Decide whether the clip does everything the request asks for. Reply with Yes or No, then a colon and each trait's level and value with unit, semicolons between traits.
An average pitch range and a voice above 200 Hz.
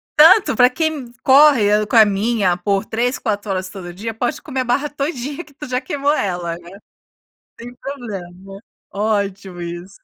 No: wide, 5.9 semitones; high, 220 Hz